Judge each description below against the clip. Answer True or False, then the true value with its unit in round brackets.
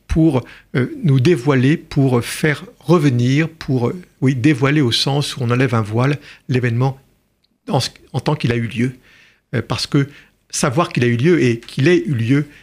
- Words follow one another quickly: False (170 wpm)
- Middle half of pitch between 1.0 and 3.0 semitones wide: False (3.6 semitones)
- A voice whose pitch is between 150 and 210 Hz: False (135 Hz)